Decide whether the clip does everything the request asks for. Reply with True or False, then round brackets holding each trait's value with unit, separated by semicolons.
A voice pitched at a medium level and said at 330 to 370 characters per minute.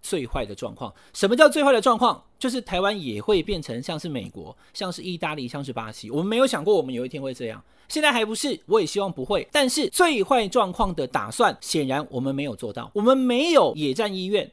False (205 Hz; 345 characters per minute)